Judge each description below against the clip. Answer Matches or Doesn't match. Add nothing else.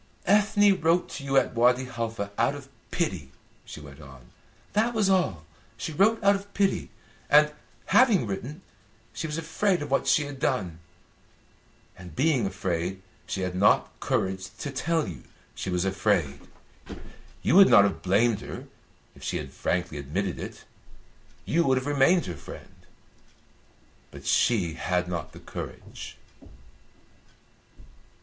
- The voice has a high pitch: Doesn't match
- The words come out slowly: Doesn't match